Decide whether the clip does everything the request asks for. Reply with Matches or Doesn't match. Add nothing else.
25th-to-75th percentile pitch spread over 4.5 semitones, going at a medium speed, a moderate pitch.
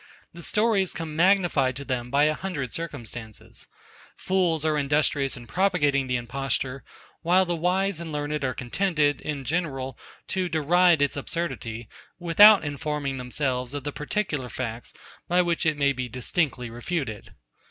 Matches